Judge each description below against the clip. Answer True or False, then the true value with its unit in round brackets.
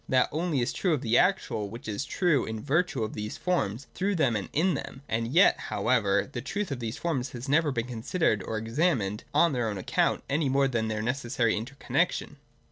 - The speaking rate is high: True (210 wpm)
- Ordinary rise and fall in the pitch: False (5.7 semitones)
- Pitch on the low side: True (125 Hz)